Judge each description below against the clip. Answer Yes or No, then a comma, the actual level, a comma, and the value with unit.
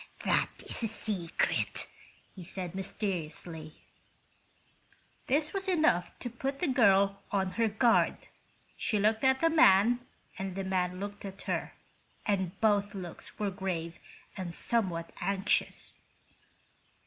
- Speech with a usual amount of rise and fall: Yes, average, 3.6 semitones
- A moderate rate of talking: No, slow, 125 wpm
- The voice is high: Yes, high, 200 Hz